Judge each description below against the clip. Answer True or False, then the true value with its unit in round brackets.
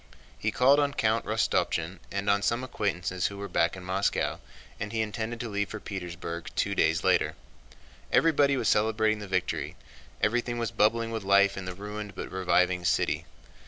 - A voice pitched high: False (105 Hz)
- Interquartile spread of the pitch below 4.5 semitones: True (3.2 semitones)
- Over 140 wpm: True (175 wpm)